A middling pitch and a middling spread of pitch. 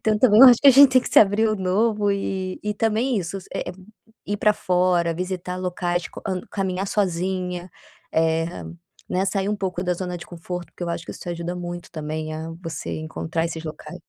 Yes: medium, 180 Hz; average, 3.0 semitones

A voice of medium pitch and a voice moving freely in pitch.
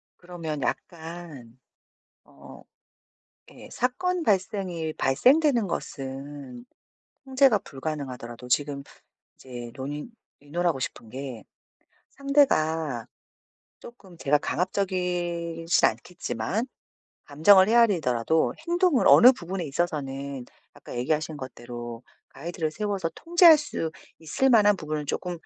Yes: medium, 160 Hz; wide, 6.5 semitones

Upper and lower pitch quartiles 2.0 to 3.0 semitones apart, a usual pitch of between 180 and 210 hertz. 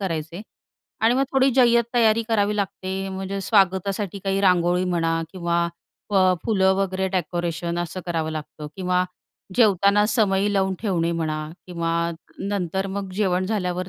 Yes: narrow, 2.6 semitones; high, 190 Hz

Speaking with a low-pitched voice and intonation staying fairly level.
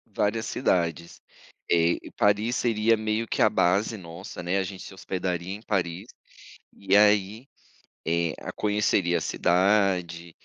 No: very low, 95 Hz; average, 3.4 semitones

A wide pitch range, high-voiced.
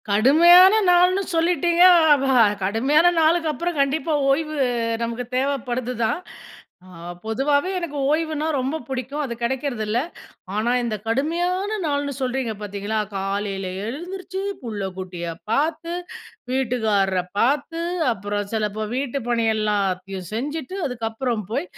Yes: wide, 6.3 semitones; very high, 260 Hz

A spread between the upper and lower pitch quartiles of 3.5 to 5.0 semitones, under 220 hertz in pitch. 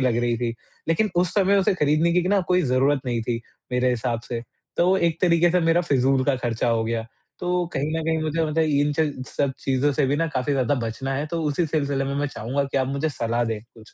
Yes: average, 4.7 semitones; medium, 140 Hz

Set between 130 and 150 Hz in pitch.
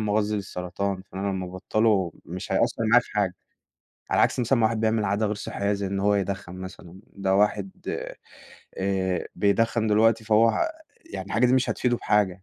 No: low, 100 Hz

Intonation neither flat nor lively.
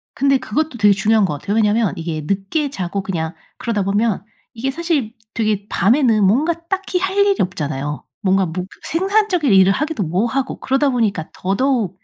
No: wide, 6.4 semitones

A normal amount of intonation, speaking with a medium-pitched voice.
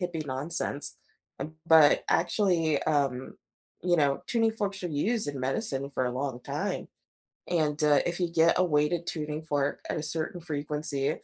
Yes: average, 3.4 semitones; medium, 155 Hz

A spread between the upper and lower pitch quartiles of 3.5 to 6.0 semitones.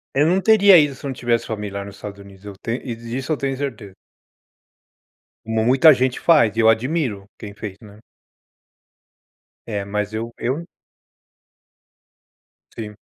Yes: average, 4.7 semitones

